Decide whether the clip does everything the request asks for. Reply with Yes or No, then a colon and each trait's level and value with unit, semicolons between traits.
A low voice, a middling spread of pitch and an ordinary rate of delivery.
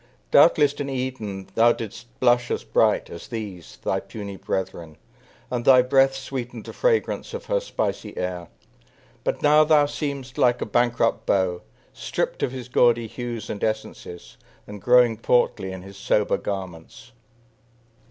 Yes: low, 120 Hz; average, 5.0 semitones; average, 150 wpm